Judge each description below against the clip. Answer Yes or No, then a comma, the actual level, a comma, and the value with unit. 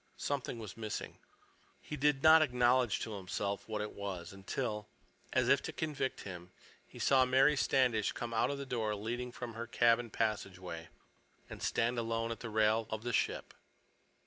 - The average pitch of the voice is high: No, low, 115 Hz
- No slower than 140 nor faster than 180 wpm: Yes, average, 175 wpm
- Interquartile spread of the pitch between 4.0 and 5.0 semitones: No, average, 3.2 semitones